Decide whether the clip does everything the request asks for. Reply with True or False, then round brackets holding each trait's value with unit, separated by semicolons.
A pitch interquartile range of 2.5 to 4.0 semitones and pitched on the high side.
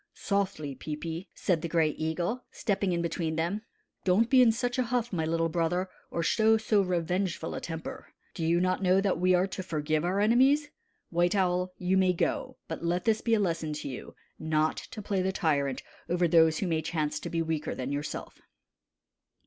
False (3.5 semitones; 175 Hz)